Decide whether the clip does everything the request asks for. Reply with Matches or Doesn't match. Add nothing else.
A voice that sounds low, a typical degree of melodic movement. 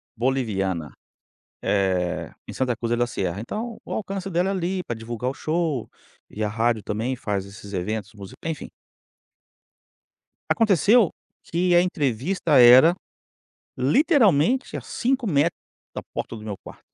Doesn't match